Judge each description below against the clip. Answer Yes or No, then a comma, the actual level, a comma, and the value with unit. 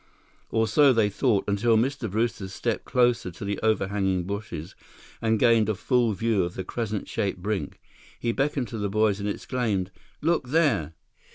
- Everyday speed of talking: Yes, average, 170 wpm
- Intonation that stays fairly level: No, average, 3.3 semitones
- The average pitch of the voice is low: Yes, low, 110 Hz